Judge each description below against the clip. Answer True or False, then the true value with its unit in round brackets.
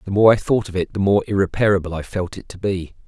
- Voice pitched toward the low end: True (95 Hz)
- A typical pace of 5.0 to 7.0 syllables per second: True (6.4 syllables/s)